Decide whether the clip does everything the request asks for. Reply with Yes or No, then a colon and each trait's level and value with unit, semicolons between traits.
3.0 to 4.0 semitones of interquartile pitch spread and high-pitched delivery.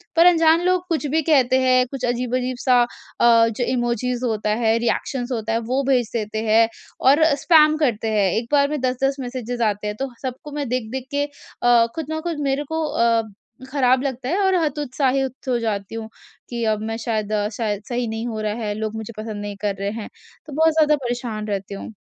Yes: average, 3.7 semitones; high, 245 Hz